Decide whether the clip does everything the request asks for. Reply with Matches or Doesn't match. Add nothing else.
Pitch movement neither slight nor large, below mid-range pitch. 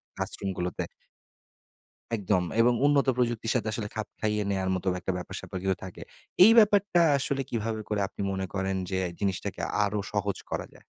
Matches